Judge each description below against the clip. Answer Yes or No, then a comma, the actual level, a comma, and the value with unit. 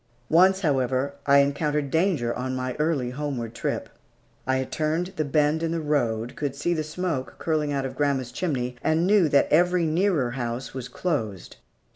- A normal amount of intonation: Yes, average, 3.9 semitones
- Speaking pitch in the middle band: Yes, medium, 145 Hz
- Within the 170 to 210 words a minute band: Yes, average, 175 wpm